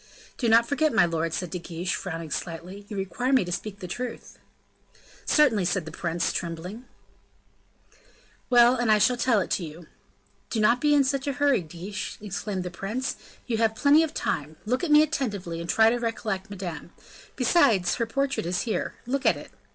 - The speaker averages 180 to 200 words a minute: Yes, average, 185 wpm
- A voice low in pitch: No, high, 215 Hz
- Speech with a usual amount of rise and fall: No, wide, 6.1 semitones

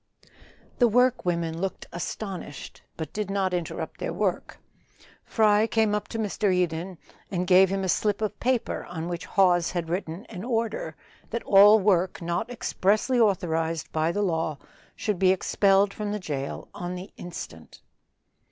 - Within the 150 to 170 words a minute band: Yes, average, 160 wpm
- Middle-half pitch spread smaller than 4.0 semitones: Yes, average, 3.5 semitones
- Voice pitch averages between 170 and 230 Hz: Yes, high, 190 Hz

